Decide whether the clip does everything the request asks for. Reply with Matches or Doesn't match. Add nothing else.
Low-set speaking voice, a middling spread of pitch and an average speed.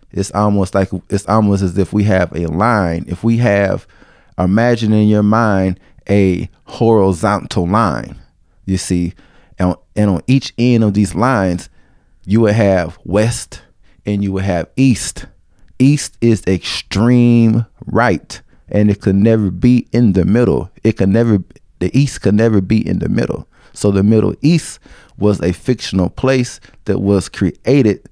Matches